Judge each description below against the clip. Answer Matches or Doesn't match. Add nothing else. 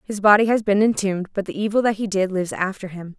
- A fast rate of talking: Matches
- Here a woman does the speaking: Matches